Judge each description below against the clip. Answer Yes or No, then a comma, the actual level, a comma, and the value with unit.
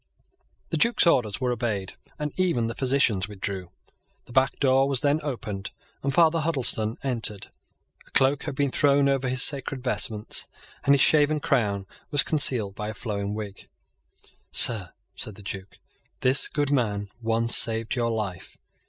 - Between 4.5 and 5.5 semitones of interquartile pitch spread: Yes, average, 4.8 semitones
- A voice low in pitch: Yes, low, 125 Hz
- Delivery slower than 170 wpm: Yes, average, 160 wpm